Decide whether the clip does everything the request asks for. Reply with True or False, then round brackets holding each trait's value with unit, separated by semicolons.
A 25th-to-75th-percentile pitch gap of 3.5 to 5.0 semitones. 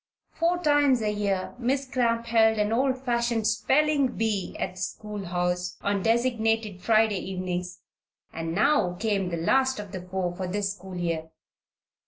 True (4.5 semitones)